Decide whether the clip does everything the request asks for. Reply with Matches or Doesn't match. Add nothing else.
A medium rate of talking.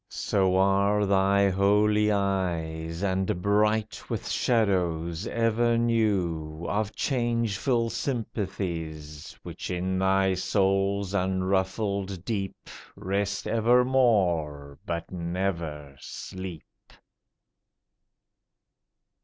Doesn't match